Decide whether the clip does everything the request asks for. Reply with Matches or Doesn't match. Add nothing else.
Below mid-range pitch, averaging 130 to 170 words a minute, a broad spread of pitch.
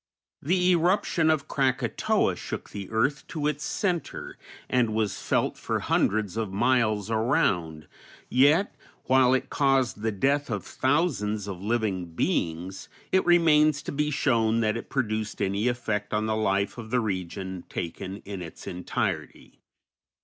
Matches